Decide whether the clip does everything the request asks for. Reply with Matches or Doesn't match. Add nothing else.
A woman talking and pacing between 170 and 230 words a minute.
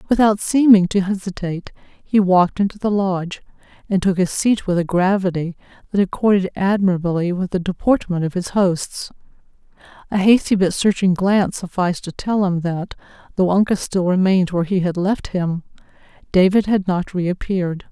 Doesn't match